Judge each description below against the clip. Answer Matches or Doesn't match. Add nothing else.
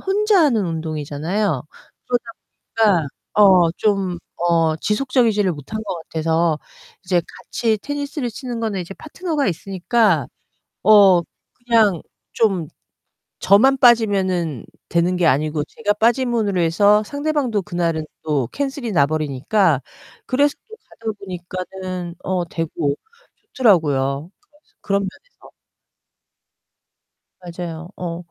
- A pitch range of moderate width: Doesn't match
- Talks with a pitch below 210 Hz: Matches